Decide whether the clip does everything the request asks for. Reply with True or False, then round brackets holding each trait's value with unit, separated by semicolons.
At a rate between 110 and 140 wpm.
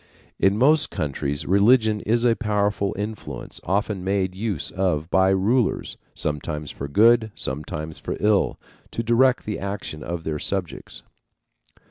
True (135 wpm)